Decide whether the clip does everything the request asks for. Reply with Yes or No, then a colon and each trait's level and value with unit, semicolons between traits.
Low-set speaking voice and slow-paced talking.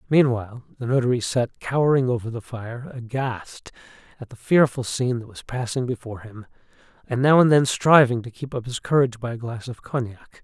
No: low, 125 Hz; average, 190 wpm